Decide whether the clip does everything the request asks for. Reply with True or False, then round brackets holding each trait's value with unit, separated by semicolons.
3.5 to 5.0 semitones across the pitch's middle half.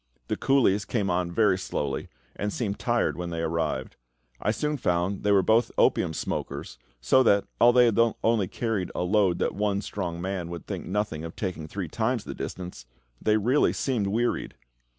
True (4.5 semitones)